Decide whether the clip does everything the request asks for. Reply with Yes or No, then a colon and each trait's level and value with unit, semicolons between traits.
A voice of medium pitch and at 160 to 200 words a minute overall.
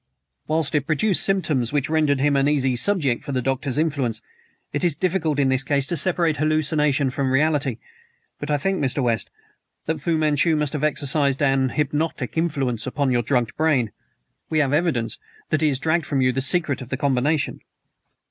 Yes: medium, 145 Hz; average, 185 wpm